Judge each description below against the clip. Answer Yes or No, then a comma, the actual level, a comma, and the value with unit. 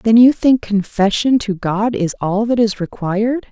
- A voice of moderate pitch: No, high, 215 Hz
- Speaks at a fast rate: No, average, 190 wpm